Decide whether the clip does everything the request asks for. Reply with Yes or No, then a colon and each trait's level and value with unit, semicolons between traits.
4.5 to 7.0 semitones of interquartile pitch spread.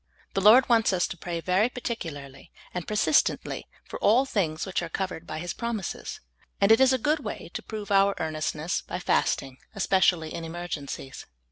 Yes: average, 5.2 semitones